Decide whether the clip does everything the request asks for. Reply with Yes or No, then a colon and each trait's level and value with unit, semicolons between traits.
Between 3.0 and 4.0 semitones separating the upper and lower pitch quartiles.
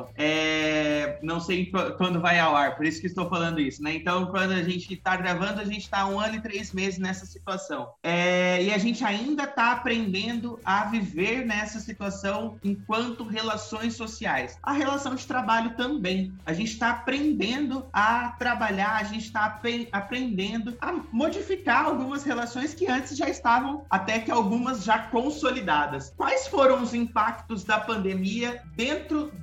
No: average, 4.5 semitones